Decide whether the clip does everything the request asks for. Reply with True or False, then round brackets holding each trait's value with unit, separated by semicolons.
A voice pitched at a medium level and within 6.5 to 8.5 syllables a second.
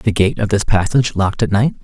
False (105 Hz; 6.9 syllables/s)